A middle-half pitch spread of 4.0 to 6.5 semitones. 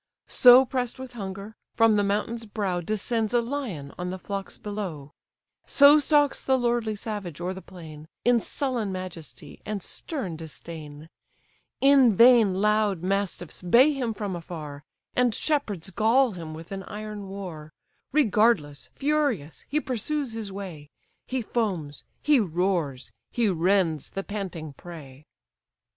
Yes: wide, 5.6 semitones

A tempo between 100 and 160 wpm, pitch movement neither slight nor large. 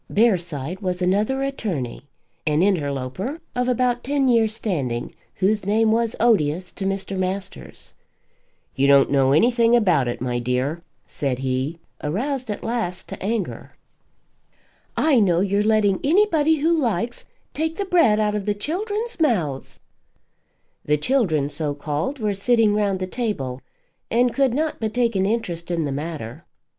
No: average, 150 wpm; wide, 7.6 semitones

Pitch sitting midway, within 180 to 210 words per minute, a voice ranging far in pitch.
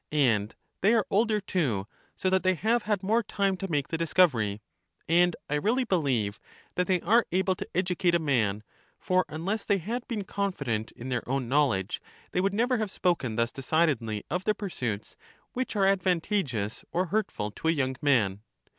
Yes: medium, 175 Hz; average, 185 wpm; wide, 7.7 semitones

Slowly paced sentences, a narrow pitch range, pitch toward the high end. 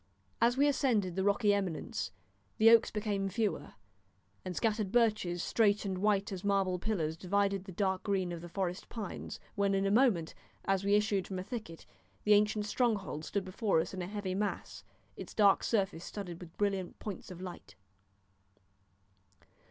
No: average, 170 wpm; narrow, 2.3 semitones; high, 200 Hz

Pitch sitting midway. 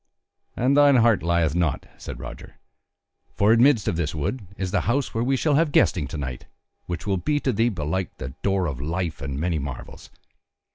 No: very low, 95 Hz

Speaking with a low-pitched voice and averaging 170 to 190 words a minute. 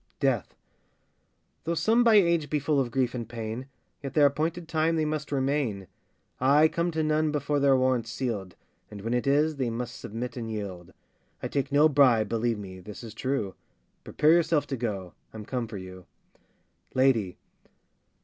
Yes: low, 130 Hz; average, 175 wpm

